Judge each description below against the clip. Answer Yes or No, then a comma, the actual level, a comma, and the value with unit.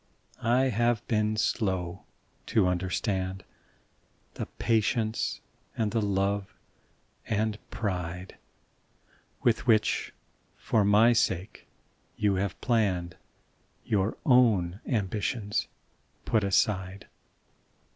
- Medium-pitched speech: No, low, 105 Hz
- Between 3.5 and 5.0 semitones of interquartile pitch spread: No, average, 2.9 semitones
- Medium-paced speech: No, slow, 85 wpm